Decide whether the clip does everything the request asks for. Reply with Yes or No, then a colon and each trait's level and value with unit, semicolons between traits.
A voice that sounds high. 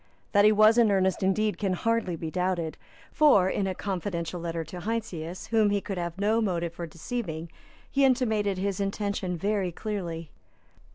Yes: high, 195 Hz